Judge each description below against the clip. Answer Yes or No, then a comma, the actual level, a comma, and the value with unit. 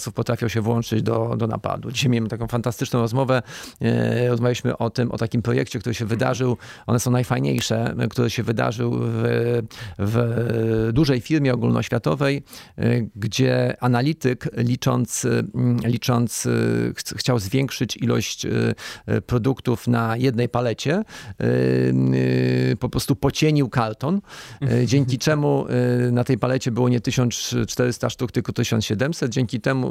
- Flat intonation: Yes, narrow, 2.0 semitones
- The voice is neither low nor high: No, low, 120 Hz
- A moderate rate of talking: Yes, average, 120 wpm